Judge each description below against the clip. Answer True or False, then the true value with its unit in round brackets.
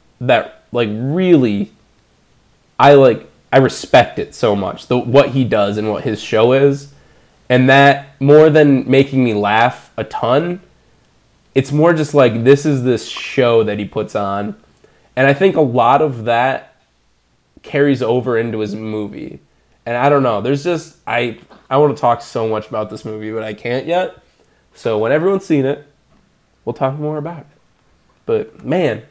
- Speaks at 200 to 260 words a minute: False (175 wpm)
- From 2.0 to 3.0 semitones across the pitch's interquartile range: False (4.5 semitones)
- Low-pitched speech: True (130 Hz)